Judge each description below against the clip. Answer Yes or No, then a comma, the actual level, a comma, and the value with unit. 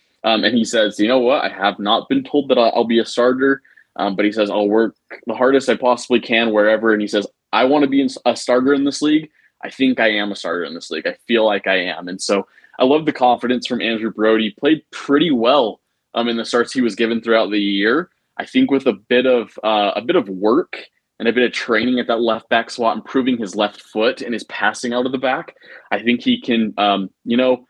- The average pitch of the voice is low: Yes, low, 120 Hz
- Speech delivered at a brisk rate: Yes, fast, 255 wpm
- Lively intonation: No, average, 3.1 semitones